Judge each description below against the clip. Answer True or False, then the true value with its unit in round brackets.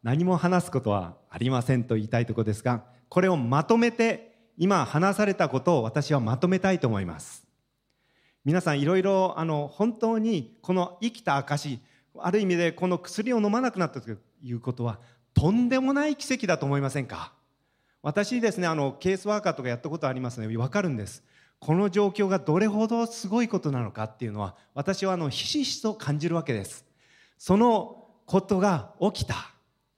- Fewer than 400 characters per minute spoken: True (370 characters per minute)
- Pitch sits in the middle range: True (170 Hz)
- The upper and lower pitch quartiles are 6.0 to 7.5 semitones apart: False (8.3 semitones)